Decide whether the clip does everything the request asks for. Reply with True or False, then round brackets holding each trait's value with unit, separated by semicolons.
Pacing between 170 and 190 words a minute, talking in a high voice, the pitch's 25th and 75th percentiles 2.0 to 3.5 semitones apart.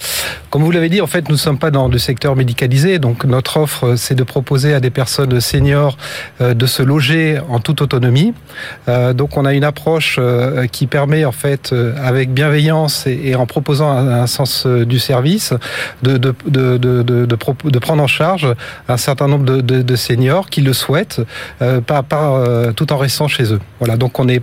False (175 wpm; 135 Hz; 2.9 semitones)